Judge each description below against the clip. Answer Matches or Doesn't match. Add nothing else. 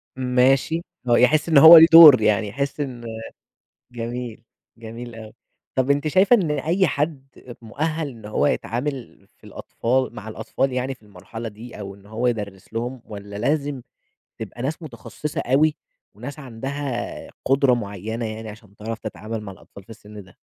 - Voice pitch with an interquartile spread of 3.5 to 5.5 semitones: Matches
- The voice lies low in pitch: Matches